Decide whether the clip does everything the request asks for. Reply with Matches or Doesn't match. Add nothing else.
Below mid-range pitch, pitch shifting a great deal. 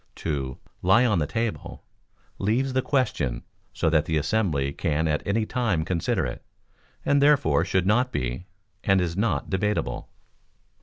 Matches